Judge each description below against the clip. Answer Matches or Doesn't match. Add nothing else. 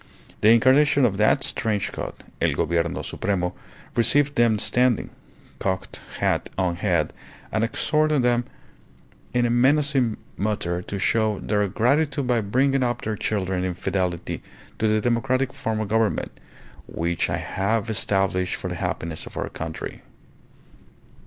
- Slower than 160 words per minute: Matches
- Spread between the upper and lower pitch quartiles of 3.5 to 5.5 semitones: Matches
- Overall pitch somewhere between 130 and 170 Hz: Doesn't match